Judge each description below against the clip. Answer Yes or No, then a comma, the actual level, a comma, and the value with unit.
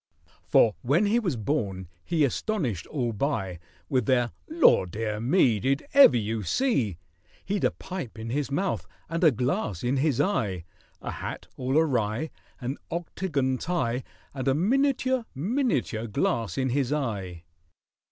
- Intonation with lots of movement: Yes, wide, 7.2 semitones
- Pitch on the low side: Yes, low, 130 Hz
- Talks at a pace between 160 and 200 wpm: No, average, 145 wpm